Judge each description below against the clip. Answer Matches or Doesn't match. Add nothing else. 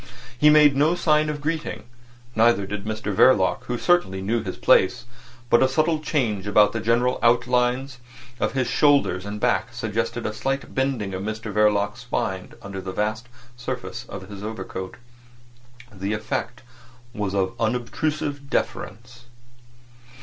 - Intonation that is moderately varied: Matches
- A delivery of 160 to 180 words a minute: Doesn't match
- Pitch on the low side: Matches